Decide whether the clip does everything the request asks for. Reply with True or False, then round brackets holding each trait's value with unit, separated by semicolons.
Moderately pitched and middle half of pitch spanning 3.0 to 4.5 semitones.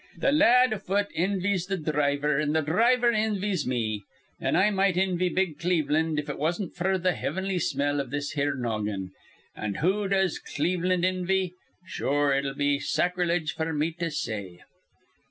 False (170 Hz; 4.9 semitones)